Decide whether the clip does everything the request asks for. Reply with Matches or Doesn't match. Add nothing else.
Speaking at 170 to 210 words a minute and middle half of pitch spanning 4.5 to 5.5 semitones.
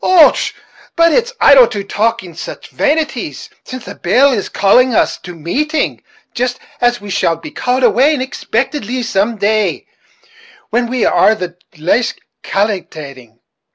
Doesn't match